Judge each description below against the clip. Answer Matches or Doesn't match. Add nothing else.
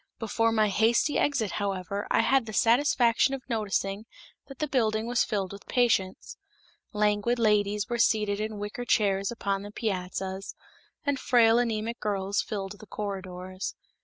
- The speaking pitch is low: Doesn't match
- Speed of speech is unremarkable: Matches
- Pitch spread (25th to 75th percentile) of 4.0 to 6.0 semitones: Doesn't match